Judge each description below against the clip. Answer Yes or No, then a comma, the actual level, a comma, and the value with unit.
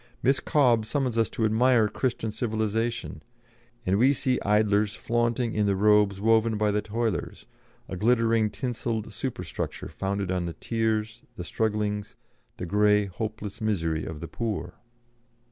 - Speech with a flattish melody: Yes, narrow, 2.1 semitones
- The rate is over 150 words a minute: No, average, 145 wpm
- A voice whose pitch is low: Yes, low, 110 Hz